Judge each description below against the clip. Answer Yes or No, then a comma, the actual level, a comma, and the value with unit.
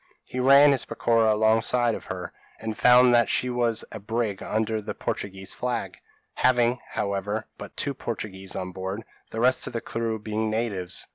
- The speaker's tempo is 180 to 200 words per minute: No, average, 170 wpm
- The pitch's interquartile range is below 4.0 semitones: Yes, average, 2.8 semitones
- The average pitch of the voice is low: Yes, low, 110 Hz